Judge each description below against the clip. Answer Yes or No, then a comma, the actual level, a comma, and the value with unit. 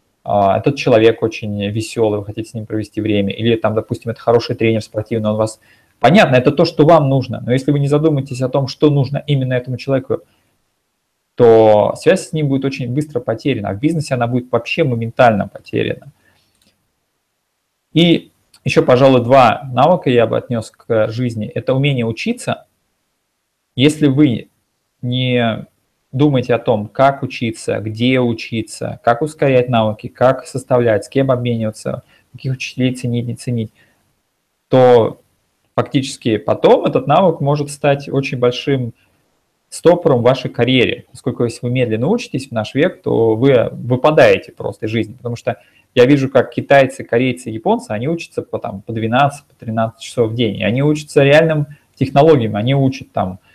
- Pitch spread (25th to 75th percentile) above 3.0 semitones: Yes, average, 3.7 semitones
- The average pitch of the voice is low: Yes, low, 125 Hz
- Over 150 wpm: Yes, fast, 160 wpm